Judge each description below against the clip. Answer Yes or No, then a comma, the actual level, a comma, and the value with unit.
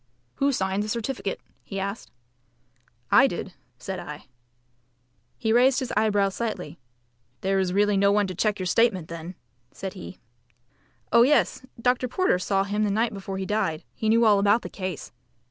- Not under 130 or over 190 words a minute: Yes, average, 170 wpm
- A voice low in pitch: No, high, 200 Hz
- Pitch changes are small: No, average, 3.2 semitones